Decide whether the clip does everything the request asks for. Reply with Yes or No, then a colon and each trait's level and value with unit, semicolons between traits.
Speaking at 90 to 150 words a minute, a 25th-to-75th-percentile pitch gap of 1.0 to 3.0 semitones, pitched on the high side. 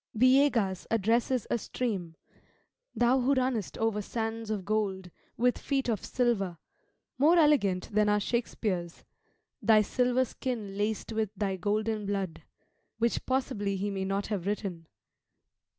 No: slow, 135 wpm; average, 3.7 semitones; high, 215 Hz